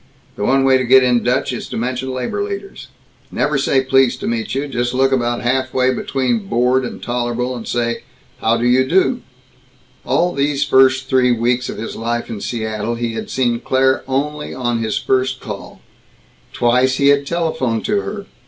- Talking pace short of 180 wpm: No, average, 185 wpm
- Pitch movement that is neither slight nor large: No, narrow, 2.0 semitones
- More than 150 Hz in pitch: No, low, 130 Hz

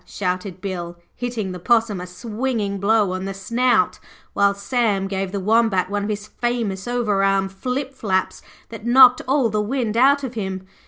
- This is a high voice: Yes, high, 210 Hz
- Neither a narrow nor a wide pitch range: Yes, average, 3.8 semitones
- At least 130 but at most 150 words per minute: No, average, 175 wpm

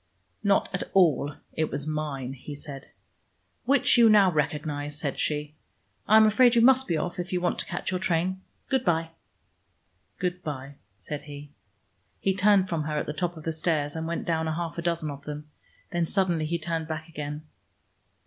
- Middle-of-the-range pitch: Yes, medium, 160 Hz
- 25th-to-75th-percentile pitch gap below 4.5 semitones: Yes, average, 3.5 semitones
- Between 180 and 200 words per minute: Yes, average, 190 wpm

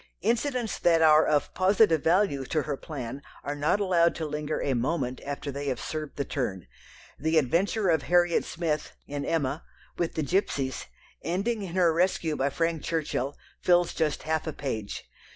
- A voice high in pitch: No, medium, 160 Hz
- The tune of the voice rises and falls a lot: No, average, 3.6 semitones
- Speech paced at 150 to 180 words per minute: Yes, average, 170 wpm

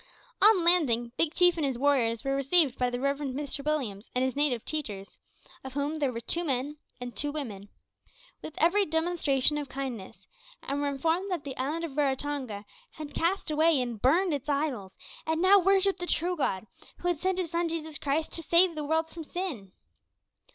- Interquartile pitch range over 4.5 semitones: No, average, 4.2 semitones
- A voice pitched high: Yes, very high, 290 Hz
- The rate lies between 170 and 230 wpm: Yes, average, 195 wpm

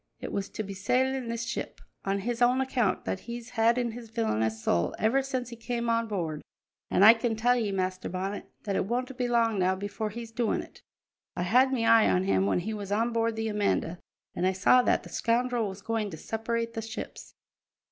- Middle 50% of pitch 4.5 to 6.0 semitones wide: No, average, 3.3 semitones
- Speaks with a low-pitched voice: No, high, 225 Hz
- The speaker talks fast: Yes, fast, 220 wpm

